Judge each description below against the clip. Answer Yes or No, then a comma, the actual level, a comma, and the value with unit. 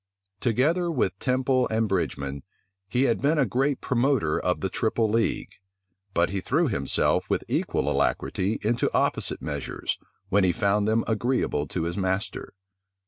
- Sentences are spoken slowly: No, average, 150 wpm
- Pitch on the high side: No, low, 110 Hz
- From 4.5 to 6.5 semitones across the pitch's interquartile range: Yes, average, 5.3 semitones